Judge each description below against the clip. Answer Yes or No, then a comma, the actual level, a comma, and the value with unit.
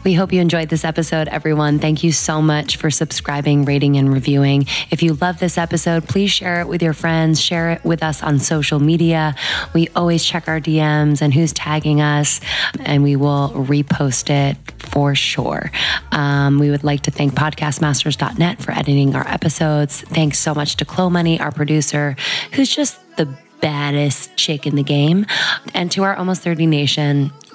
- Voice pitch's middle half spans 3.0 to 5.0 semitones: No, narrow, 2.5 semitones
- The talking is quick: No, average, 180 wpm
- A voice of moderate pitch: Yes, medium, 155 Hz